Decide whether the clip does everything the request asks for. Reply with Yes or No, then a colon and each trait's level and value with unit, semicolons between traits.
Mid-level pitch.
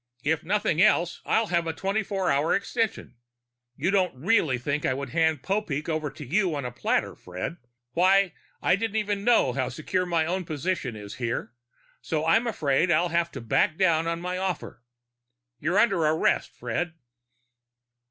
Yes: medium, 170 Hz